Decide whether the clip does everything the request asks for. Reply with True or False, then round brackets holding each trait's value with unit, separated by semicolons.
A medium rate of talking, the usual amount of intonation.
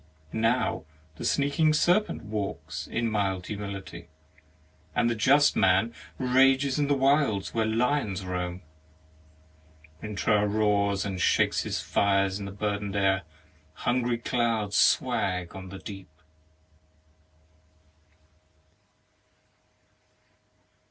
False (100 wpm; 4.1 semitones)